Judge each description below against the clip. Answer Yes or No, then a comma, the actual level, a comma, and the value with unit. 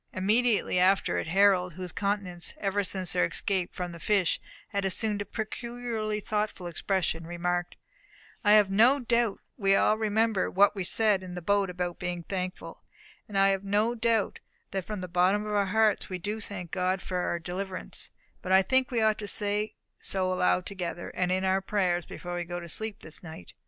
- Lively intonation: No, average, 2.7 semitones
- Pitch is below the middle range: No, high, 195 Hz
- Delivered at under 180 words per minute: No, average, 195 wpm